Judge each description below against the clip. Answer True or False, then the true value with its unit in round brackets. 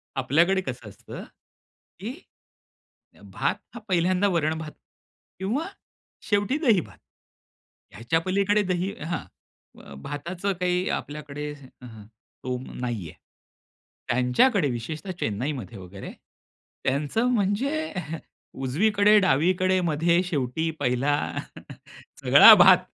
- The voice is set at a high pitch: False (165 Hz)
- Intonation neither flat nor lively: False (7.0 semitones)